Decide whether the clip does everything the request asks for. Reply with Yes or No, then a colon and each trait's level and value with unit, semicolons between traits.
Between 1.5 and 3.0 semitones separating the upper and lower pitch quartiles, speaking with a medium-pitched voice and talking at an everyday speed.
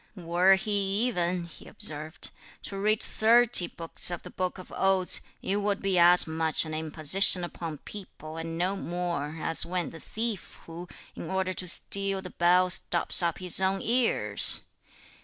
Yes: narrow, 2.5 semitones; medium, 180 Hz; average, 165 wpm